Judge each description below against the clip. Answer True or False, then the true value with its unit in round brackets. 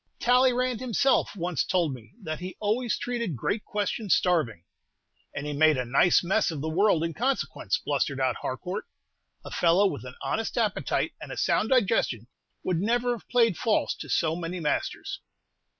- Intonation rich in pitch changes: True (6.7 semitones)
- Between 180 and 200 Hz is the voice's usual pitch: True (185 Hz)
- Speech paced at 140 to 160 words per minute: False (170 wpm)